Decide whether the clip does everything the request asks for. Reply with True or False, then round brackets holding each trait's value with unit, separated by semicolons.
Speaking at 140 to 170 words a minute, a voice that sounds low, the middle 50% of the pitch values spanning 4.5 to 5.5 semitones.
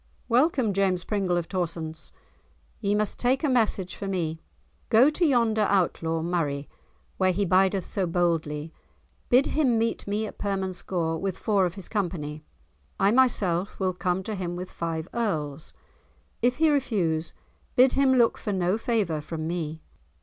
False (155 wpm; 190 Hz; 4.9 semitones)